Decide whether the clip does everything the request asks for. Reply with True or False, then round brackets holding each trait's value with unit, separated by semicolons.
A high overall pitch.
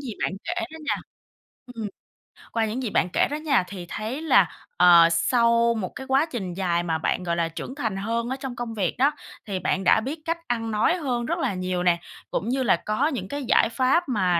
True (230 Hz)